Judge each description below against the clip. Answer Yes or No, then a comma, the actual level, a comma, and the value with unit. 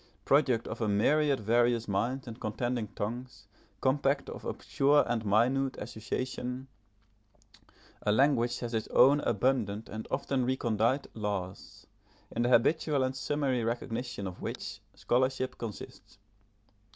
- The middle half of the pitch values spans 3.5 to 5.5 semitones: No, average, 3.1 semitones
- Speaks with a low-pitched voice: Yes, low, 120 Hz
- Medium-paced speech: No, slow, 125 wpm